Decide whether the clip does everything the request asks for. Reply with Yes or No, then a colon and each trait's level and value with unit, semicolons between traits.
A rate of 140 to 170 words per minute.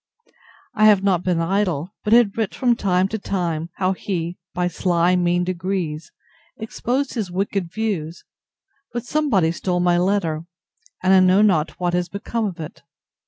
Yes: average, 165 wpm